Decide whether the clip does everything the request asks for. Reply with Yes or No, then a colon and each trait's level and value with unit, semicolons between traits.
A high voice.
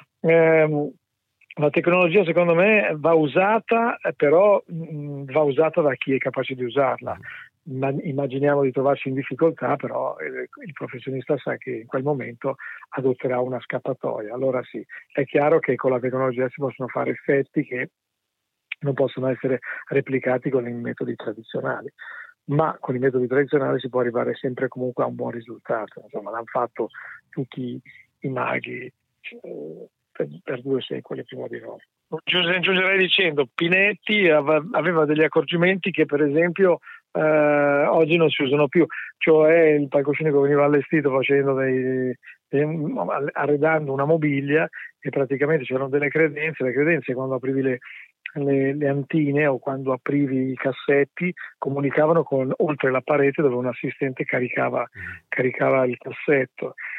No: medium, 140 Hz